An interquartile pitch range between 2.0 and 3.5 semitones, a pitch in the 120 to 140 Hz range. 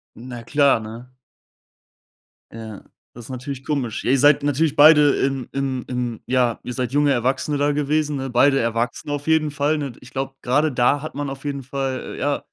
Yes: average, 2.7 semitones; low, 135 Hz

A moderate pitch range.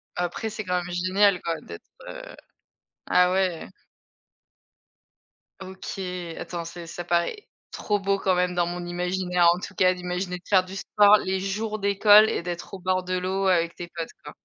No: narrow, 1.8 semitones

